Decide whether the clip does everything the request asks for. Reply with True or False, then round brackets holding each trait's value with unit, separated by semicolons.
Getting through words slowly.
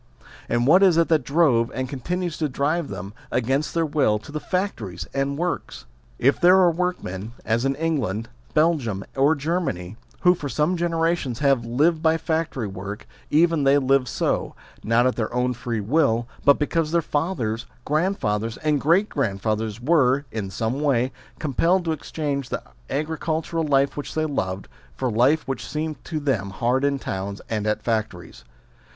False (170 wpm)